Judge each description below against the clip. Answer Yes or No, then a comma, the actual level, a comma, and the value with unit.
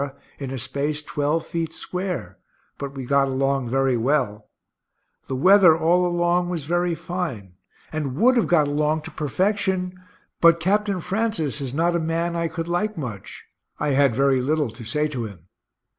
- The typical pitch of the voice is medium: Yes, medium, 155 Hz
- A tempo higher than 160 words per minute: Yes, average, 170 wpm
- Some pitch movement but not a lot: Yes, average, 4.4 semitones